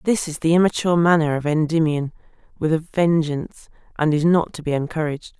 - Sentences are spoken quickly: No, average, 180 wpm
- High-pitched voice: No, medium, 160 Hz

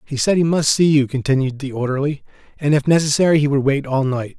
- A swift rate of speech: Yes, fast, 235 wpm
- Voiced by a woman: No, male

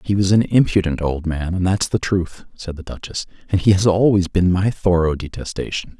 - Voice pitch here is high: No, very low, 90 Hz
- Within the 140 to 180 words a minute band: No, average, 200 wpm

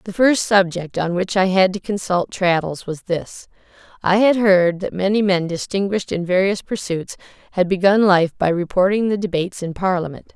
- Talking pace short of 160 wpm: No, average, 175 wpm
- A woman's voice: Yes, female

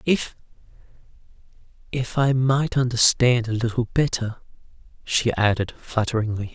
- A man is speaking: Yes, male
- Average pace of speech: No, slow, 90 wpm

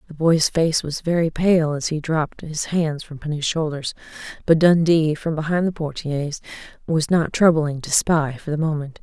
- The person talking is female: Yes, female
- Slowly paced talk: No, average, 185 wpm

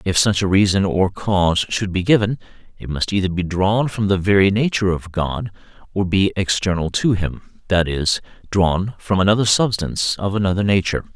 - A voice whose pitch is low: Yes, very low, 95 Hz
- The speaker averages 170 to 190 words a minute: Yes, average, 180 wpm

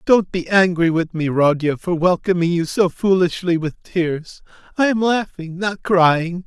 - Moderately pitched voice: Yes, medium, 175 Hz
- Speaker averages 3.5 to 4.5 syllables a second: Yes, 4.2 syllables/s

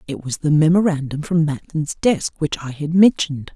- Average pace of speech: Yes, average, 185 wpm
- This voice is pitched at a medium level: Yes, medium, 155 Hz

